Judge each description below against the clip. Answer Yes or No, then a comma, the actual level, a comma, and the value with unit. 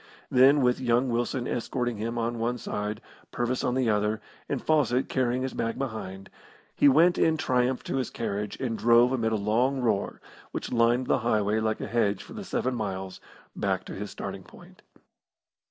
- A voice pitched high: No, low, 120 Hz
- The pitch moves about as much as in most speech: Yes, average, 3.0 semitones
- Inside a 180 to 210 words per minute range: Yes, average, 185 wpm